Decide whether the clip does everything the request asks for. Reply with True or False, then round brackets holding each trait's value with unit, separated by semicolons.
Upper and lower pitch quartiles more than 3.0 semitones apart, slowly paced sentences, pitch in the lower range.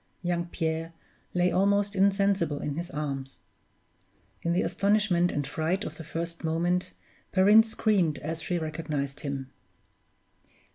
False (3.7 semitones; 130 wpm; 170 Hz)